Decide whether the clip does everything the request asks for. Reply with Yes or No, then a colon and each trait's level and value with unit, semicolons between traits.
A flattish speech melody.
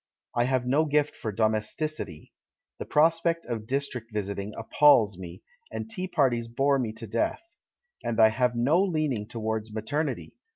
No: average, 5.3 semitones